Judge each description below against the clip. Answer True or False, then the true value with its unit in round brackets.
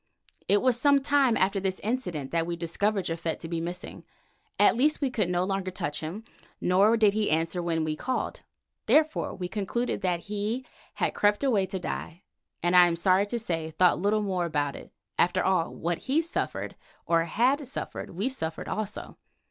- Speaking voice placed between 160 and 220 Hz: True (190 Hz)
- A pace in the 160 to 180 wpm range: False (190 wpm)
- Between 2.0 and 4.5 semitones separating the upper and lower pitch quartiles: False (4.9 semitones)